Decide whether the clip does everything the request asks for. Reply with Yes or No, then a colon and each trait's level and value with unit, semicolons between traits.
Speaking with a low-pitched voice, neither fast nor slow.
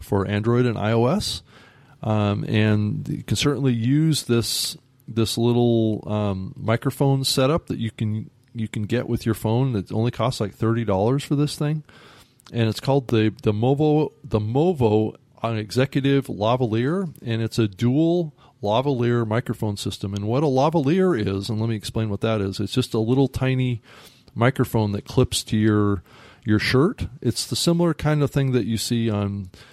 Yes: low, 120 Hz; average, 175 wpm